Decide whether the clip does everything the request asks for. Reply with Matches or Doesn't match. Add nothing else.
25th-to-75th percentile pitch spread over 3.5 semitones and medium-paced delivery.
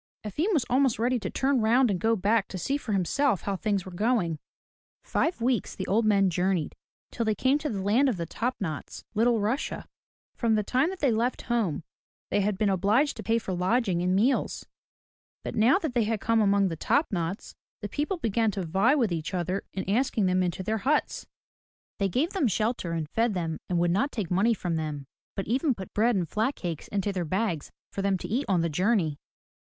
Doesn't match